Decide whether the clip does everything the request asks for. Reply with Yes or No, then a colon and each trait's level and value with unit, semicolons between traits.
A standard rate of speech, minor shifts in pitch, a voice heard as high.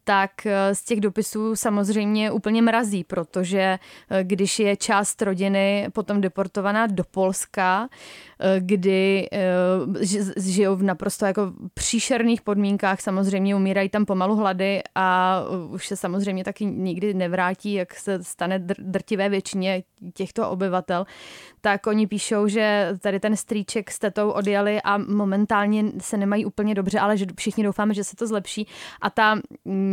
Yes: average, 135 wpm; narrow, 1.6 semitones; high, 200 Hz